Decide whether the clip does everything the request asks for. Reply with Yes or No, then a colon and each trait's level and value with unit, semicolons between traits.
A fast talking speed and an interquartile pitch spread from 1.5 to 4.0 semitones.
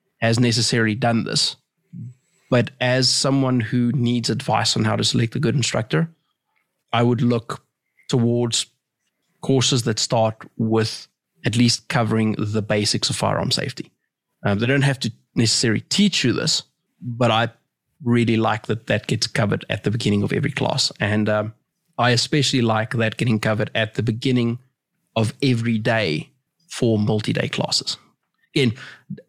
No: average, 150 wpm; average, 2.7 semitones